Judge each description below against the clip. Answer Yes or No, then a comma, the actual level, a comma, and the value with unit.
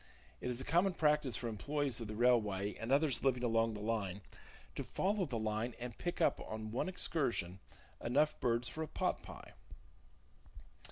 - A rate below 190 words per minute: Yes, average, 175 wpm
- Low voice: Yes, low, 120 Hz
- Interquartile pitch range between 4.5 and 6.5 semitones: Yes, average, 5.1 semitones